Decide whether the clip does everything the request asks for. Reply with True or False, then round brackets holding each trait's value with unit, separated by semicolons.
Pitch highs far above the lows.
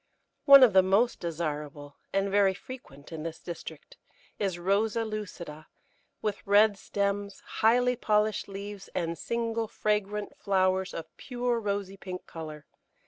False (3.7 semitones)